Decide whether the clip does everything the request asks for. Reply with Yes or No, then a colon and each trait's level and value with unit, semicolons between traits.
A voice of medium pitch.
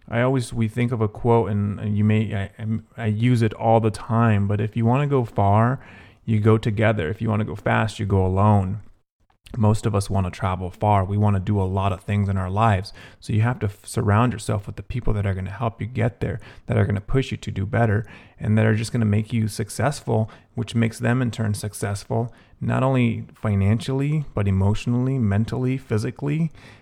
No: low, 110 Hz